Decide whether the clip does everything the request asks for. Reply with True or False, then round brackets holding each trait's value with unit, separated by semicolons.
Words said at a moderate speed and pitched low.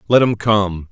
True (195 wpm; 105 Hz)